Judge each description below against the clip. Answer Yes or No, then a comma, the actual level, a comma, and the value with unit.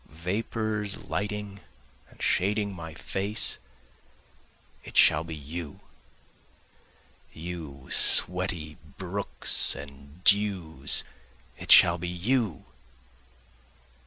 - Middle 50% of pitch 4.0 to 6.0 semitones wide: Yes, average, 4.4 semitones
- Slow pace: Yes, slow, 80 wpm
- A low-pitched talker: Yes, very low, 90 Hz